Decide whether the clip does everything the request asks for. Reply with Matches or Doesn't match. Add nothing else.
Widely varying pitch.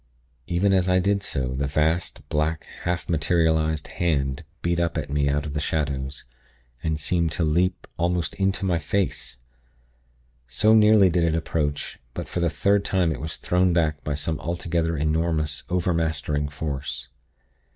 Doesn't match